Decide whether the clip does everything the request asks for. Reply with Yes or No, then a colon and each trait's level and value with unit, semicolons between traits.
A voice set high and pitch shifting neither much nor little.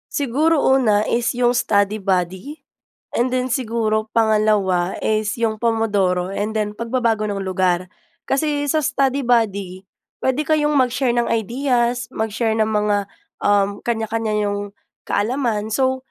Yes: high, 225 Hz; average, 3.5 semitones